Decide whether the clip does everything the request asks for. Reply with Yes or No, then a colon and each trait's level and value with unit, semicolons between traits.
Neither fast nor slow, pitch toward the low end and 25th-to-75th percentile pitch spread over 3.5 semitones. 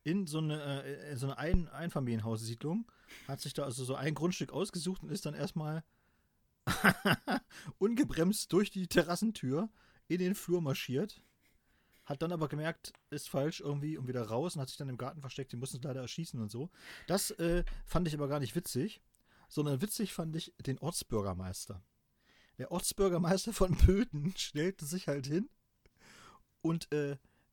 No: average, 165 wpm; medium, 150 Hz; average, 4.7 semitones